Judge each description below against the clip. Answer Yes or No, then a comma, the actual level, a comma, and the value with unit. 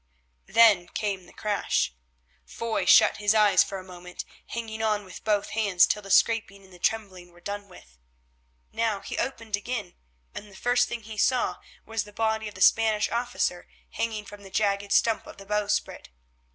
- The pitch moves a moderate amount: No, narrow, 2.2 semitones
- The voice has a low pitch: No, high, 210 Hz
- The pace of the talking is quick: No, average, 185 wpm